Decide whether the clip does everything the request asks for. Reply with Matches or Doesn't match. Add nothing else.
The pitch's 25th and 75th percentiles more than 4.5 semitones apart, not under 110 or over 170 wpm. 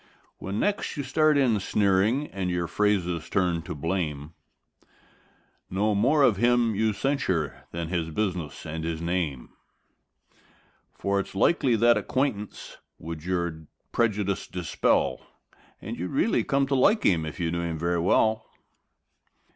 Matches